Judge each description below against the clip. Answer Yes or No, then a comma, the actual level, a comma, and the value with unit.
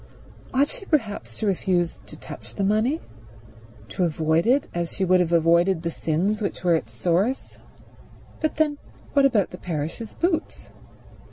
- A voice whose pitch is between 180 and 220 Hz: Yes, high, 190 Hz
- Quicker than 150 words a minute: Yes, average, 160 wpm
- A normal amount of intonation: No, wide, 6.5 semitones